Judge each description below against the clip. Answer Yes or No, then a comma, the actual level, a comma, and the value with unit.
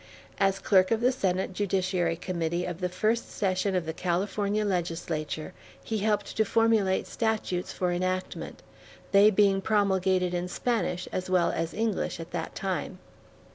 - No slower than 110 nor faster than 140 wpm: No, average, 150 wpm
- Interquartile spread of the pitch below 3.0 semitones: Yes, narrow, 2.5 semitones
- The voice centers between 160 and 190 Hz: Yes, medium, 185 Hz